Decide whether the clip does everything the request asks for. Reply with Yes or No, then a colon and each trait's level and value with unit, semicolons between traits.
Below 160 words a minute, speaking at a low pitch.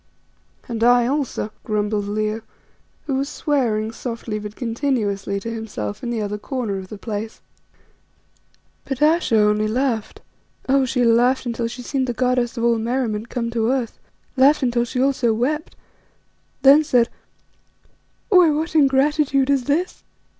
No: average, 145 wpm; high, 240 Hz